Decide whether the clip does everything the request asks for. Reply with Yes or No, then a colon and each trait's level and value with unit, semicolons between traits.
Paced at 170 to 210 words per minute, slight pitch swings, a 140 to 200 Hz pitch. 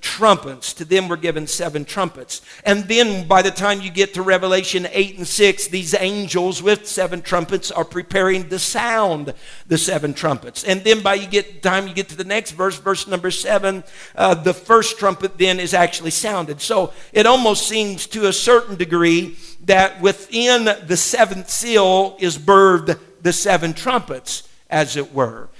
Yes: average, 175 wpm; narrow, 2.3 semitones; high, 190 Hz